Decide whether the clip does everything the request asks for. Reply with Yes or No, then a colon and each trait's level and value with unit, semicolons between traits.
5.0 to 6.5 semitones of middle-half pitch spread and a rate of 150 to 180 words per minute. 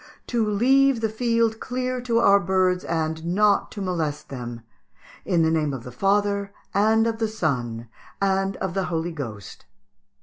Yes: wide, 5.6 semitones; average, 165 wpm